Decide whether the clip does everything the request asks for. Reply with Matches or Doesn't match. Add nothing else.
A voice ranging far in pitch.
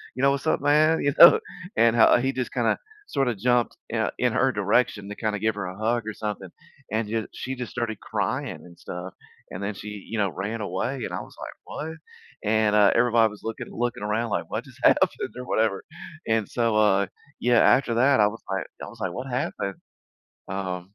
Doesn't match